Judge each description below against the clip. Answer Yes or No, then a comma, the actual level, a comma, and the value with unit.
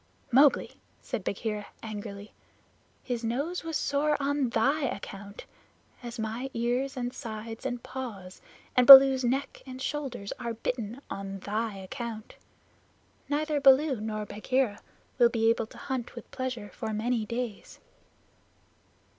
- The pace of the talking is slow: Yes, slow, 130 wpm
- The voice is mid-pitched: No, high, 240 Hz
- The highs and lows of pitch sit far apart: No, average, 3.6 semitones